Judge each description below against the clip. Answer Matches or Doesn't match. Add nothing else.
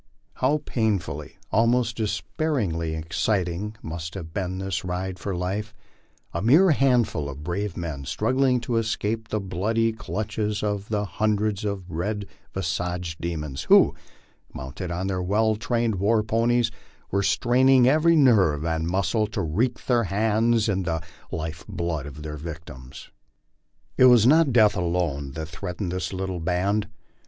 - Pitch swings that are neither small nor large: Matches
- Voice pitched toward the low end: Matches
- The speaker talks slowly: Doesn't match